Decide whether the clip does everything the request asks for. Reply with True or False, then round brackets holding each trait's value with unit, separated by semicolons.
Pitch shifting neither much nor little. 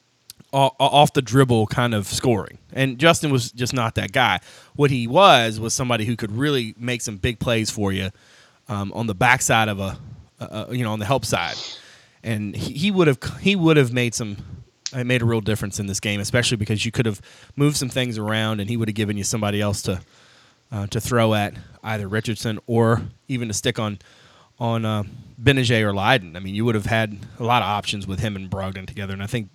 True (3.1 semitones)